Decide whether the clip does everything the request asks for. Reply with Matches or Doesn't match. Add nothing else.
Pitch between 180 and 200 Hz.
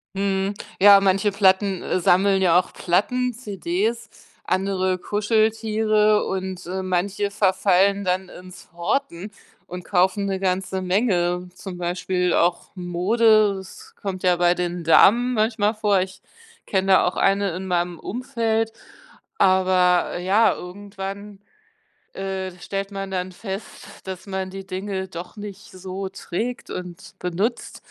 Matches